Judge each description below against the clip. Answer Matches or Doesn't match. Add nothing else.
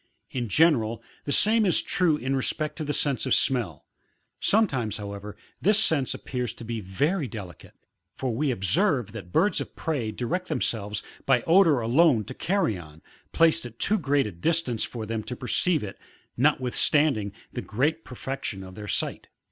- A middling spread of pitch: Doesn't match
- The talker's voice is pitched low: Matches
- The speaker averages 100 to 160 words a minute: Doesn't match